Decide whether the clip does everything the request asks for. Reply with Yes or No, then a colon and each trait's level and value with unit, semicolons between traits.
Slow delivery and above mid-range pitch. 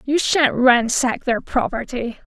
Yes: slow, 130 wpm; very high, 255 Hz